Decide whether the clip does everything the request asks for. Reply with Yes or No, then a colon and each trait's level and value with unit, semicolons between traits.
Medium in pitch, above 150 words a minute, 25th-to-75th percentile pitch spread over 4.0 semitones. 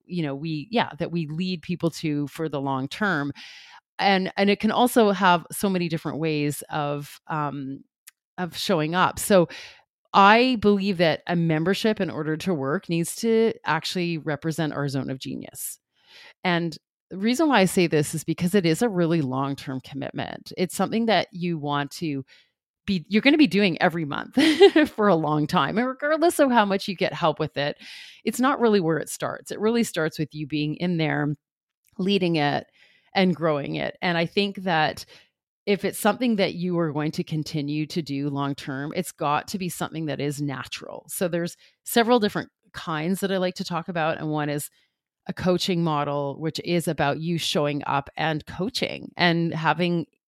Yes: medium, 170 Hz; average, 190 wpm; average, 4.6 semitones